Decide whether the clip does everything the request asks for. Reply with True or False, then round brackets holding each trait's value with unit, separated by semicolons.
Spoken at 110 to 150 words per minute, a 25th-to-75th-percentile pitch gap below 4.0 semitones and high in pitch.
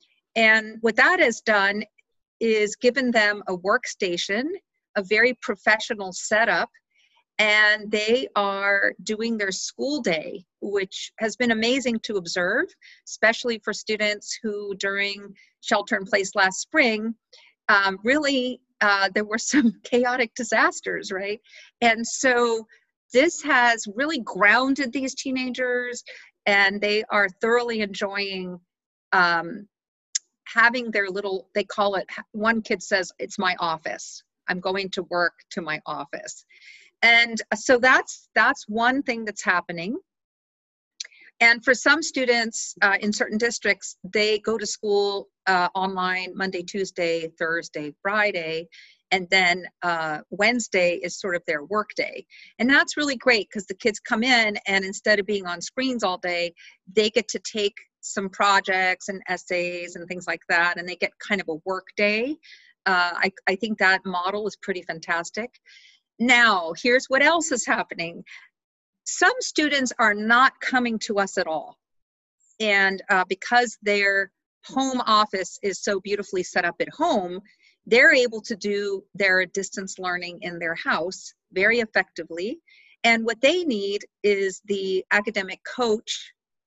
False (145 wpm; 4.3 semitones; 210 Hz)